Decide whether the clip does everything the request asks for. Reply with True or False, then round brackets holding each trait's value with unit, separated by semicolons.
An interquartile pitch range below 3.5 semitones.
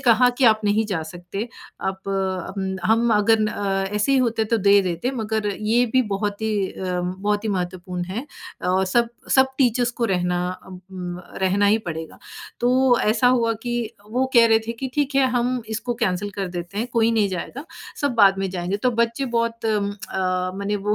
False (3.8 semitones)